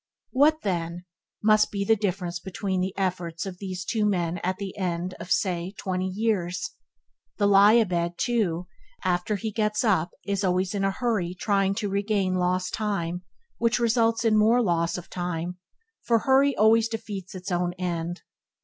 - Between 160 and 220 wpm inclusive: Yes, average, 170 wpm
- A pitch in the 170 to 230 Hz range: Yes, high, 190 Hz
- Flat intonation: No, average, 3.2 semitones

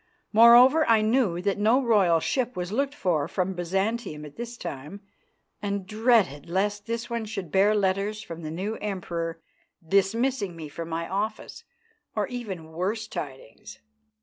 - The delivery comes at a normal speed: Yes, average, 150 wpm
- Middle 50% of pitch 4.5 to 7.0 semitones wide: Yes, average, 5.0 semitones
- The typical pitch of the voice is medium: No, high, 200 Hz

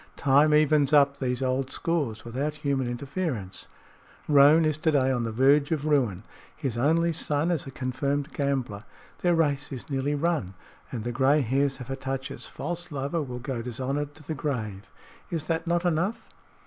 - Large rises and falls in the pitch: No, average, 3.0 semitones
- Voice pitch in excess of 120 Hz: Yes, medium, 140 Hz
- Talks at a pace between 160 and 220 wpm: Yes, average, 175 wpm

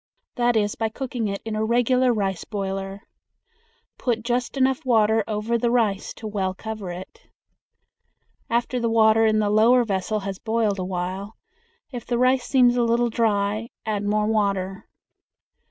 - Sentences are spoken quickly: No, average, 160 wpm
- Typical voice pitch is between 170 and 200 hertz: No, high, 220 Hz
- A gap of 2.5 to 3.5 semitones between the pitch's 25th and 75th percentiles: Yes, average, 2.9 semitones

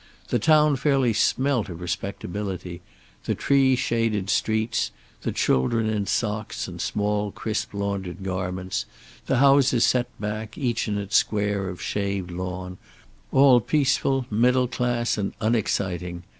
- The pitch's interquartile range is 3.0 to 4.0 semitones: No, average, 4.4 semitones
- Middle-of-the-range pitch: No, low, 105 Hz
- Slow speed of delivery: Yes, slow, 130 wpm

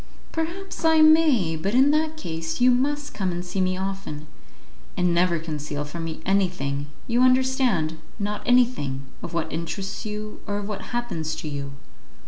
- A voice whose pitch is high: Yes, high, 195 Hz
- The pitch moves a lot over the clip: Yes, wide, 7.8 semitones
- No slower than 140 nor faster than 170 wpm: Yes, average, 165 wpm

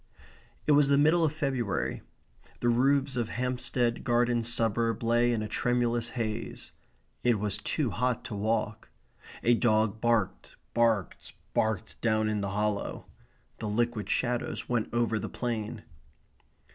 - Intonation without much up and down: Yes, narrow, 2.2 semitones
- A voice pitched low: Yes, low, 115 Hz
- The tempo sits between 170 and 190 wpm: No, average, 140 wpm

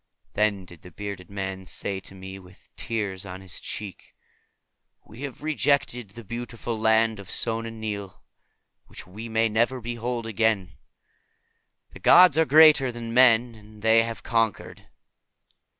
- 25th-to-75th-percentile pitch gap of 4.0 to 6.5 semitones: No, average, 3.1 semitones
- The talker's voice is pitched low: Yes, low, 110 Hz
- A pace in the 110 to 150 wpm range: Yes, average, 145 wpm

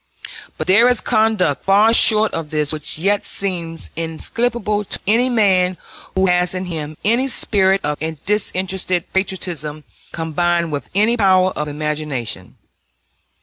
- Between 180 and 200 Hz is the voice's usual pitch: Yes, medium, 185 Hz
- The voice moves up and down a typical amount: Yes, average, 4.5 semitones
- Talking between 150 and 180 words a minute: No, slow, 135 wpm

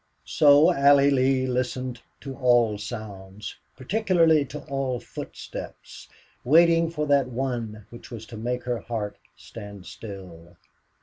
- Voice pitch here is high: No, low, 125 Hz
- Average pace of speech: No, slow, 125 wpm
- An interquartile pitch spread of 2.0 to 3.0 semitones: No, average, 4.5 semitones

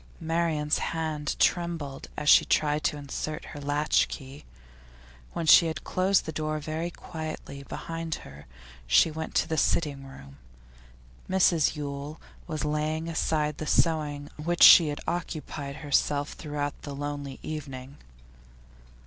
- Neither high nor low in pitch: Yes, medium, 150 Hz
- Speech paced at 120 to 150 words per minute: Yes, average, 140 wpm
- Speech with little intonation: Yes, narrow, 1.9 semitones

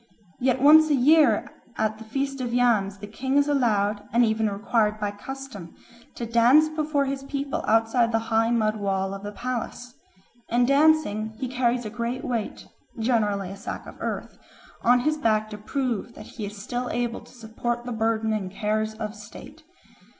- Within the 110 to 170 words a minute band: No, average, 180 wpm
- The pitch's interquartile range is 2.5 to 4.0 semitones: Yes, average, 3.3 semitones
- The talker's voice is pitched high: Yes, high, 230 Hz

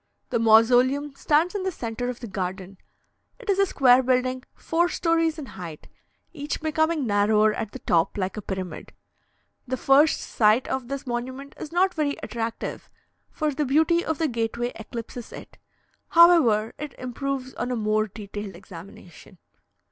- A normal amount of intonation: No, wide, 5.8 semitones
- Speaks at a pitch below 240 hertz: No, very high, 250 Hz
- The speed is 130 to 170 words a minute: Yes, average, 160 wpm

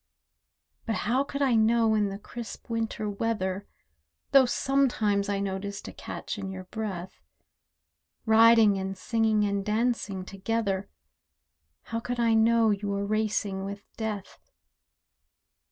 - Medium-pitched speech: No, high, 215 Hz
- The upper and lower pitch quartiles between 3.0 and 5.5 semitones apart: No, narrow, 2.4 semitones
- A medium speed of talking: No, slow, 130 wpm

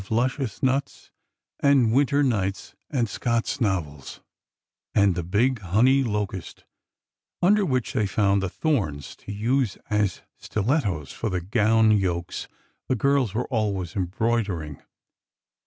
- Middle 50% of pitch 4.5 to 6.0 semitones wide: Yes, average, 5.2 semitones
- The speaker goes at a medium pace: No, slow, 130 wpm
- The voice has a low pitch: Yes, low, 110 Hz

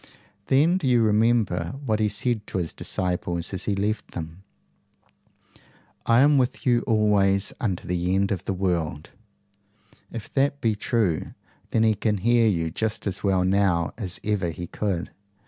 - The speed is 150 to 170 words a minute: Yes, average, 165 wpm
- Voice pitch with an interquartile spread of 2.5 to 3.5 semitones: No, average, 4.0 semitones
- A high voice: No, low, 105 Hz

